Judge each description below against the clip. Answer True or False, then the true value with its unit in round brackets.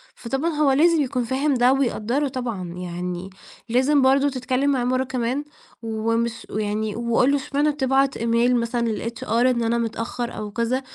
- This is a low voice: False (245 Hz)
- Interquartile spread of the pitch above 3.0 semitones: False (2.7 semitones)